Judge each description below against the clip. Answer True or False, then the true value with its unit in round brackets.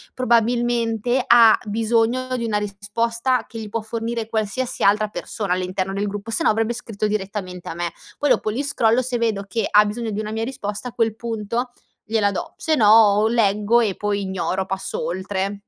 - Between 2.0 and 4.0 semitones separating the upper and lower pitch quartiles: True (2.5 semitones)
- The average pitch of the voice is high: True (220 Hz)